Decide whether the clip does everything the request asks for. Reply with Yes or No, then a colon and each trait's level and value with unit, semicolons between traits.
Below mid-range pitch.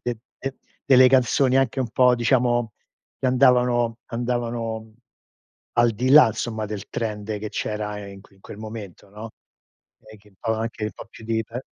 Yes: low, 115 Hz